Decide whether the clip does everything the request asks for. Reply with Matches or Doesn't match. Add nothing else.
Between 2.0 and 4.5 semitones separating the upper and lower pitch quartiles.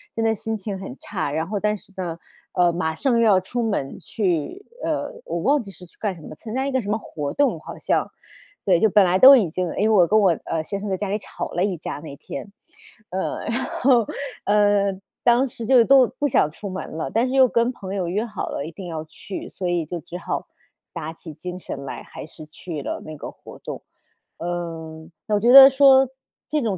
Doesn't match